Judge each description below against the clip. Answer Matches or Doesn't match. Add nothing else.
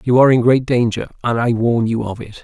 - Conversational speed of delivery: Doesn't match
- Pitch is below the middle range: Matches